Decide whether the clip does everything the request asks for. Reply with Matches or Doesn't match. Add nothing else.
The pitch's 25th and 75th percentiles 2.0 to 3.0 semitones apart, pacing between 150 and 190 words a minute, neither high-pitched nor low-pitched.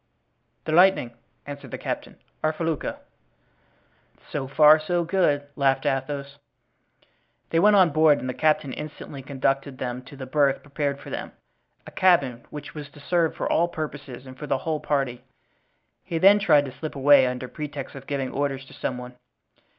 Matches